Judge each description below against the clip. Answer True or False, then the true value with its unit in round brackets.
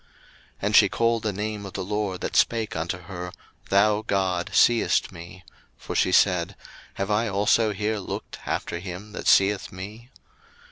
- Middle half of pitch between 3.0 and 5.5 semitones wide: False (2.5 semitones)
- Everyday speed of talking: True (170 wpm)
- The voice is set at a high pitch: False (100 Hz)